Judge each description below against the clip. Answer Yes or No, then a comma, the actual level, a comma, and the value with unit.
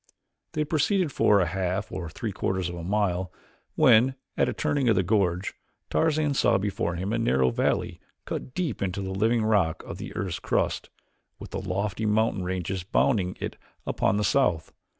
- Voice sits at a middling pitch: No, low, 100 Hz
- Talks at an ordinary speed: Yes, average, 180 wpm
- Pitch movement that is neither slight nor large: Yes, average, 4.0 semitones